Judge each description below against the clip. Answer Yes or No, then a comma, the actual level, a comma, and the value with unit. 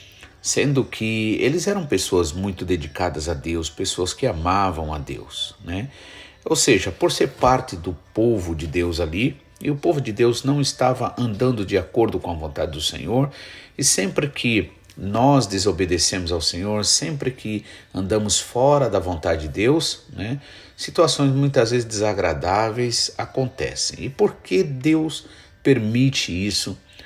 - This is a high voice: No, low, 105 Hz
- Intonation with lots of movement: Yes, wide, 6.1 semitones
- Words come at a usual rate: Yes, average, 150 wpm